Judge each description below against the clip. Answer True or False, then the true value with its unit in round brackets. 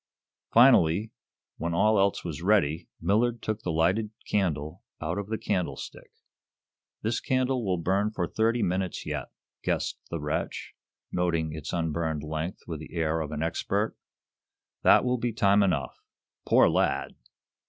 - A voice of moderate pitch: False (90 Hz)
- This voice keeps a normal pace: True (145 wpm)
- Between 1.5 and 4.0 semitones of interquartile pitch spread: False (5.0 semitones)